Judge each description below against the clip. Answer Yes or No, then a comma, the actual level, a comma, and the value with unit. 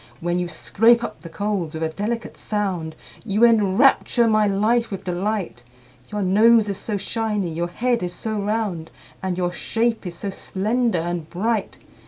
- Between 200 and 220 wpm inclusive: No, average, 170 wpm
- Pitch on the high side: Yes, high, 200 Hz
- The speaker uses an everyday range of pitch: Yes, average, 4.1 semitones